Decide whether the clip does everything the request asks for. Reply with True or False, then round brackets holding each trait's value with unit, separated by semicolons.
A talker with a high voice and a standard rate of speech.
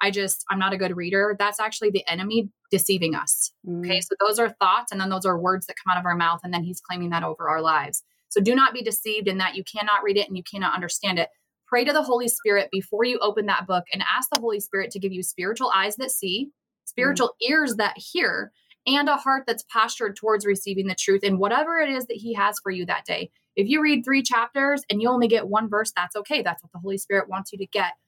False (205 Hz; 260 wpm)